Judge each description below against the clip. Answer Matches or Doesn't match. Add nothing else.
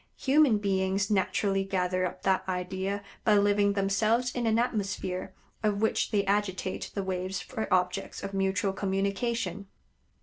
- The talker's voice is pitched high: Matches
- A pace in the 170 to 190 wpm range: Doesn't match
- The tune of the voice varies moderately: Doesn't match